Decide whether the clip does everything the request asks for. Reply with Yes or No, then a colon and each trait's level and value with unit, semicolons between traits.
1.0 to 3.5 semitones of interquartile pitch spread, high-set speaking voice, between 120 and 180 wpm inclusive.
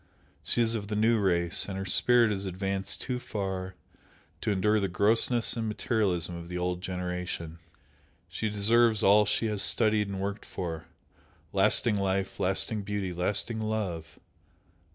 No: average, 3.0 semitones; low, 100 Hz; average, 155 wpm